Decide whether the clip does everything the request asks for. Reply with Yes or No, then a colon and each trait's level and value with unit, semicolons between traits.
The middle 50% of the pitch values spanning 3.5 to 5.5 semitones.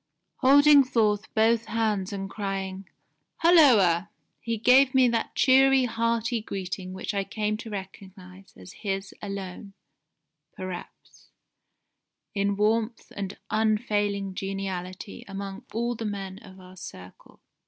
No: average, 3.0 semitones